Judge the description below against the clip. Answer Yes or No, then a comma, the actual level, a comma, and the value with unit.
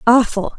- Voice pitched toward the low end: No, high, 230 Hz